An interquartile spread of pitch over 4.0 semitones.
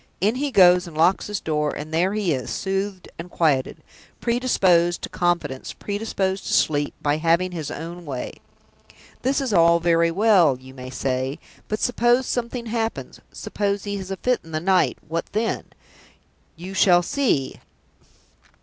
Yes: average, 4.5 semitones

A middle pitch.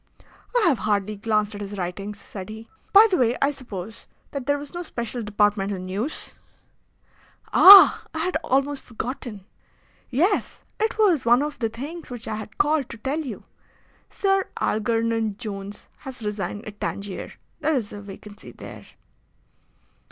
No: high, 230 Hz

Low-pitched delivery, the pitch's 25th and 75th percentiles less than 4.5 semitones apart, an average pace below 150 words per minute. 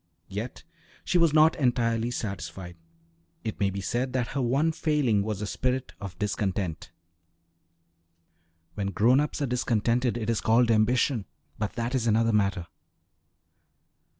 Yes: low, 115 Hz; average, 3.8 semitones; average, 140 wpm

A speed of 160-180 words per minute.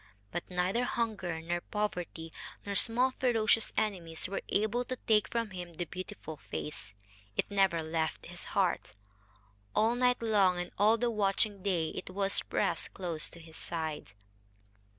No: average, 150 wpm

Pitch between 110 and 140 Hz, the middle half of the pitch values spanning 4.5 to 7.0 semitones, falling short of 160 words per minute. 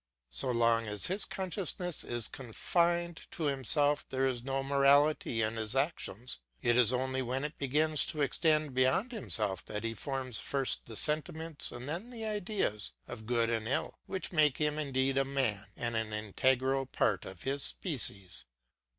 No: low, 135 Hz; average, 4.8 semitones; average, 170 wpm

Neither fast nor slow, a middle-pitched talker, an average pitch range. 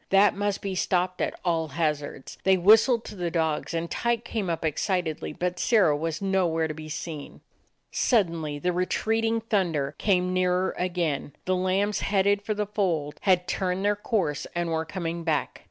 Yes: average, 175 wpm; medium, 180 Hz; average, 3.6 semitones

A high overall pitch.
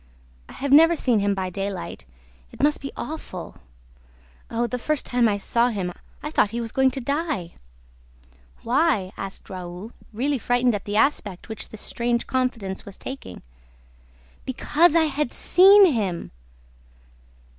Yes: high, 235 Hz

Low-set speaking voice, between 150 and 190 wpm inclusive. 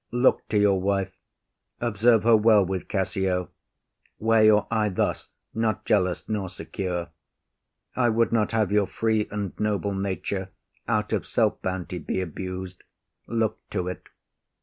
No: low, 100 Hz; average, 140 wpm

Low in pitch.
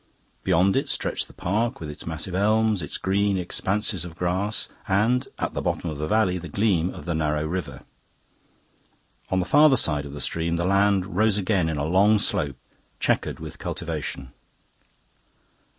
Yes: very low, 95 Hz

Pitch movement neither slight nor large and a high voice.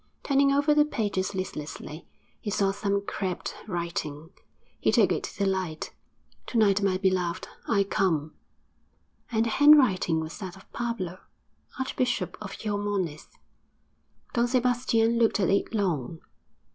Yes: average, 4.4 semitones; high, 200 Hz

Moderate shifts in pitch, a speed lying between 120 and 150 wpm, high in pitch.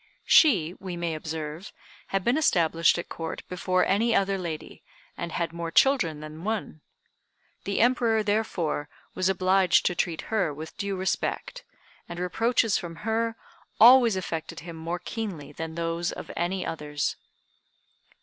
No: average, 4.4 semitones; average, 145 wpm; medium, 180 Hz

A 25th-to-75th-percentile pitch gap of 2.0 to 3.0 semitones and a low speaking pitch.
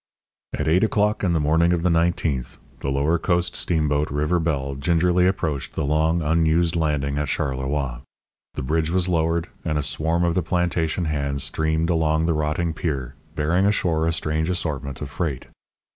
Yes: average, 2.7 semitones; very low, 80 Hz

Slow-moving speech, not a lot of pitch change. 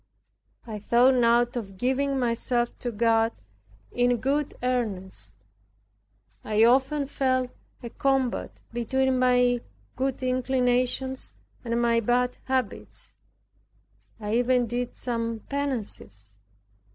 Yes: slow, 105 wpm; narrow, 1.9 semitones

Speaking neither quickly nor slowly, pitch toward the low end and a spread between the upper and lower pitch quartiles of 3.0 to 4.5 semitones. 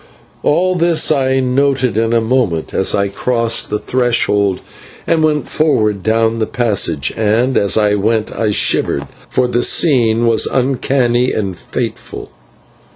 Yes: average, 145 wpm; low, 115 Hz; average, 3.8 semitones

